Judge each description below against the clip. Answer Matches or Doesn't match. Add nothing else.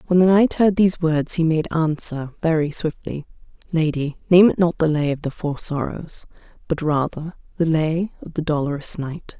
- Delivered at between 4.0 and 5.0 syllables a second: Matches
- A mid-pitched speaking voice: Matches